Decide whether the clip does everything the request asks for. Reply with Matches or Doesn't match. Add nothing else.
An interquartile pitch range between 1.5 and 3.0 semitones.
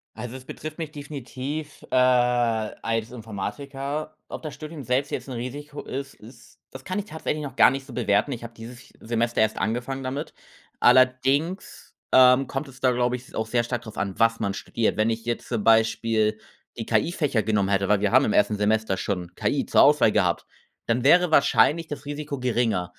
Doesn't match